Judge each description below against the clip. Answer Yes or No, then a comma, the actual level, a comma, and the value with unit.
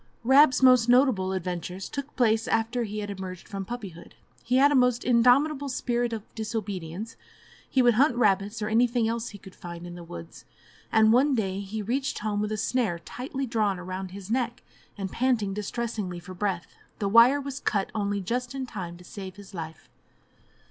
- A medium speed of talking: Yes, average, 185 wpm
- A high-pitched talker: Yes, high, 220 Hz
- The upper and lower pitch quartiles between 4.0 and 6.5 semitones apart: Yes, average, 4.3 semitones